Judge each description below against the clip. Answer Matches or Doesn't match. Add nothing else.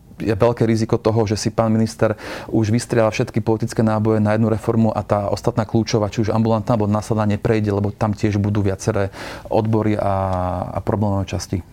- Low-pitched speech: Matches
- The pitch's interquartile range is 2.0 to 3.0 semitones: Doesn't match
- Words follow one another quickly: Matches